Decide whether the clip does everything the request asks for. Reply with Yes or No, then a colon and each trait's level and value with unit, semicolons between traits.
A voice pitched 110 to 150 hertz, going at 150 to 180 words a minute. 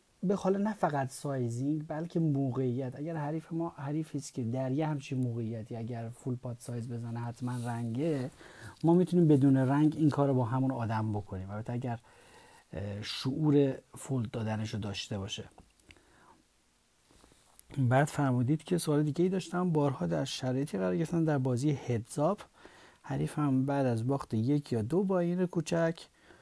Yes: low, 135 Hz; fast, 155 wpm